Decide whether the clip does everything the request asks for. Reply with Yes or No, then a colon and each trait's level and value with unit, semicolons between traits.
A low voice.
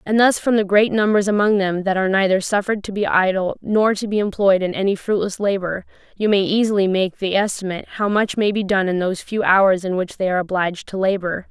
No: high, 195 Hz